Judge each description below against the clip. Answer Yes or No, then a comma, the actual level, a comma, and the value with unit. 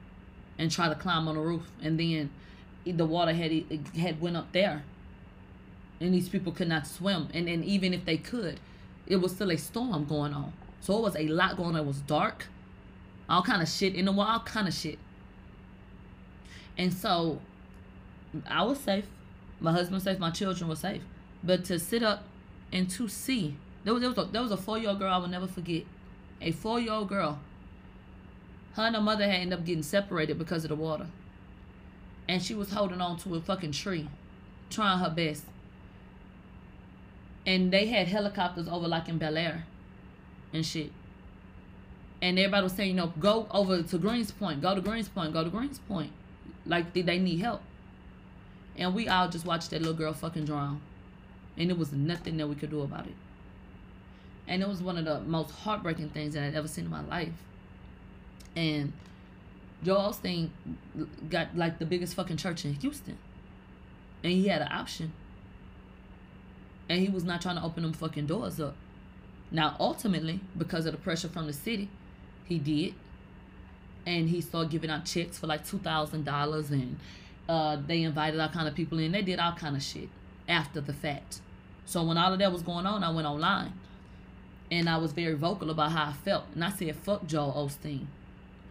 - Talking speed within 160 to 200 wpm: Yes, average, 190 wpm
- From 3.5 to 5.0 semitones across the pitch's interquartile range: Yes, average, 4.6 semitones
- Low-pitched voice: No, medium, 165 Hz